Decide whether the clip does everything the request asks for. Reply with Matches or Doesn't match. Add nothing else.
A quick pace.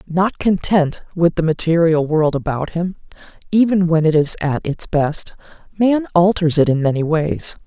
Doesn't match